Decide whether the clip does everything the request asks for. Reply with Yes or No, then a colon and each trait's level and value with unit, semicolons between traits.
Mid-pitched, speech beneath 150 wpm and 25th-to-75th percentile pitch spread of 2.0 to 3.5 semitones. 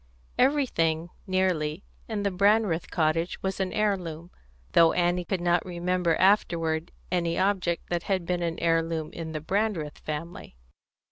Yes: medium, 175 Hz; average, 140 wpm; narrow, 2.6 semitones